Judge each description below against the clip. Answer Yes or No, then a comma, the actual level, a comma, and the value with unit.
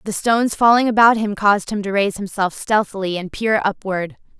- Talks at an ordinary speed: Yes, average, 190 wpm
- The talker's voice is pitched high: Yes, high, 205 Hz